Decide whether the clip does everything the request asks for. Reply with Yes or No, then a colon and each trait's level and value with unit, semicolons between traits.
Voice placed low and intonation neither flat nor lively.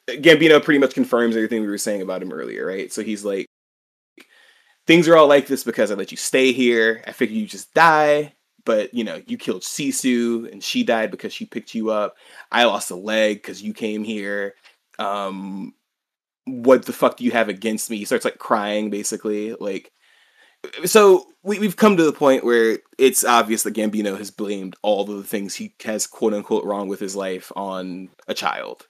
No: low, 115 Hz; wide, 6.1 semitones